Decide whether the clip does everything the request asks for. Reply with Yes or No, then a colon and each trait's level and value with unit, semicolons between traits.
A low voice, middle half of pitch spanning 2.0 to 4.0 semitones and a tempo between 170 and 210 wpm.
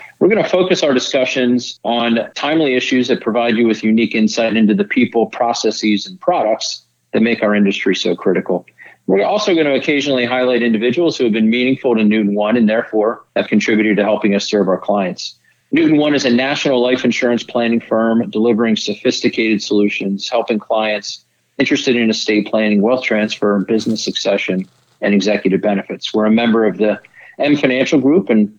Yes: low, 115 Hz; average, 3.1 semitones; average, 180 wpm